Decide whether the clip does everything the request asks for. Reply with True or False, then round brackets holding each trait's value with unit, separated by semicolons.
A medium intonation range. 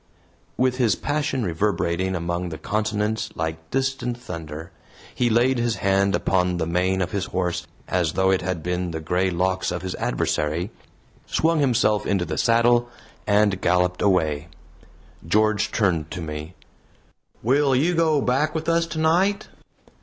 False (5.8 semitones)